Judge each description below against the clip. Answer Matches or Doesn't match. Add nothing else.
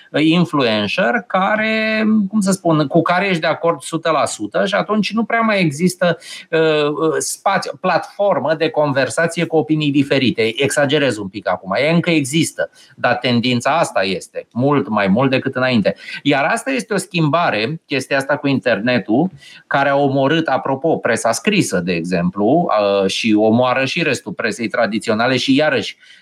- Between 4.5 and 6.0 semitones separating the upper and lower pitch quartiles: Matches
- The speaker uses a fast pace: Doesn't match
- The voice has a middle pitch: Matches